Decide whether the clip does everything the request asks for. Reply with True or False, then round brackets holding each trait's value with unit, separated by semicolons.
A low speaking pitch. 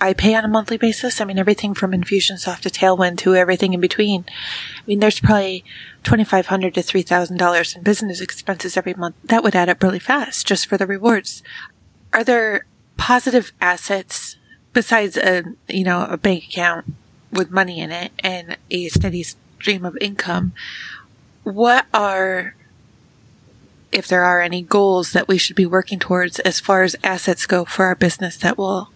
False (190 Hz)